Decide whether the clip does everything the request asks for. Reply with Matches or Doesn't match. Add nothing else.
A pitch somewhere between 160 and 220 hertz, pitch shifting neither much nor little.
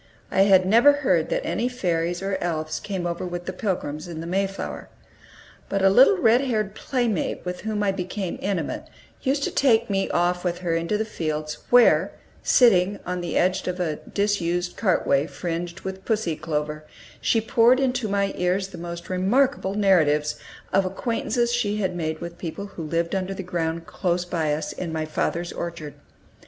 Matches